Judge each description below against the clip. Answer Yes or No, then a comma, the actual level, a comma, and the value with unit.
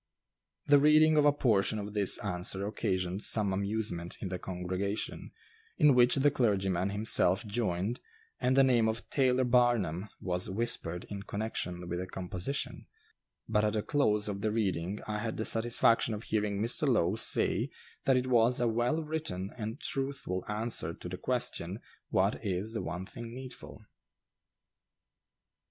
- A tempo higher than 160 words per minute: No, average, 155 wpm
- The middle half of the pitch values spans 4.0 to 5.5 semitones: Yes, average, 4.3 semitones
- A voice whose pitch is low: Yes, low, 105 Hz